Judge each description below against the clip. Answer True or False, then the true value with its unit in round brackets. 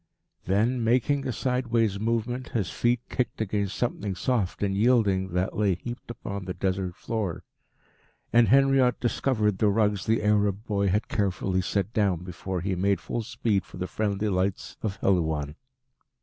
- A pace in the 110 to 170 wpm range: True (160 wpm)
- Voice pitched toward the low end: True (105 Hz)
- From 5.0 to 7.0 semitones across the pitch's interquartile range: False (3.5 semitones)